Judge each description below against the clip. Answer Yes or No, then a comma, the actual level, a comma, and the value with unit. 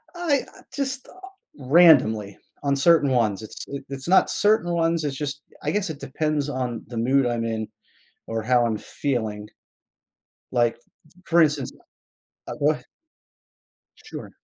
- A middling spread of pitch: No, wide, 5.7 semitones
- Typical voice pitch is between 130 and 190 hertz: Yes, medium, 140 Hz